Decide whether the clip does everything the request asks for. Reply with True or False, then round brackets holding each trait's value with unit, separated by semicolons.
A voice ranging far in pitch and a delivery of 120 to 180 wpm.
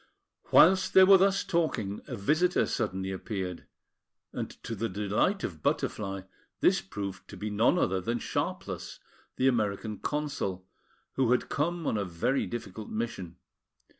True (7.5 semitones; 145 wpm)